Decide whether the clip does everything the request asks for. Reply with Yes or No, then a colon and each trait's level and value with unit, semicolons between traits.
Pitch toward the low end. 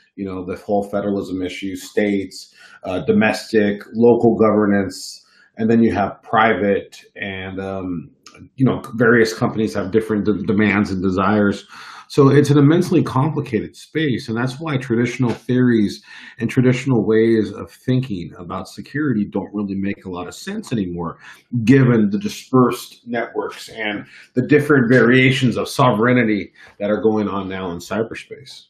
Yes: low, 110 Hz